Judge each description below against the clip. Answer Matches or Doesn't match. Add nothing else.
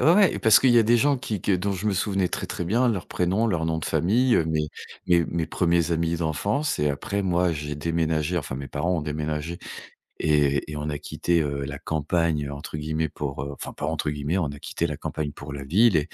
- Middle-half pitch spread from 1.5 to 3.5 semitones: Doesn't match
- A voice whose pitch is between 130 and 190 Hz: Doesn't match